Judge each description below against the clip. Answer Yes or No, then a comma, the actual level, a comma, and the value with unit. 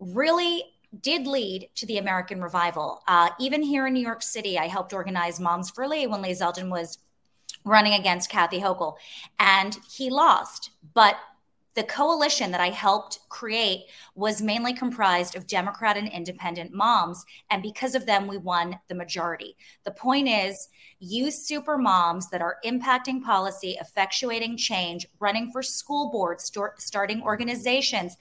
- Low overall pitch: No, high, 200 Hz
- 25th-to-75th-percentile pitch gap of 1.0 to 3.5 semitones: No, average, 5.2 semitones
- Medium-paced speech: Yes, average, 155 wpm